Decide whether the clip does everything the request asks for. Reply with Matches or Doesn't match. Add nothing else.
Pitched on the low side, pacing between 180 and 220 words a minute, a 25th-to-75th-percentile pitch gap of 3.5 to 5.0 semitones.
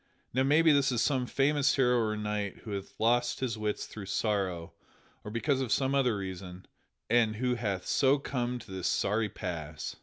Matches